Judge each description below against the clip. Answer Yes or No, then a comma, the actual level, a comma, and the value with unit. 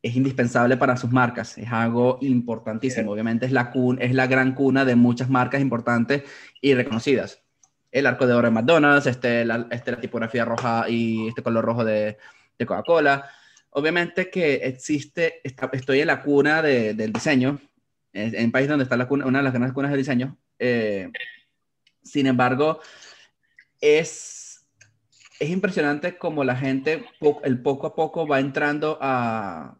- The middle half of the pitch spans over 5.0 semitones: No, average, 3.0 semitones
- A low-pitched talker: Yes, low, 130 Hz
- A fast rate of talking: No, average, 165 wpm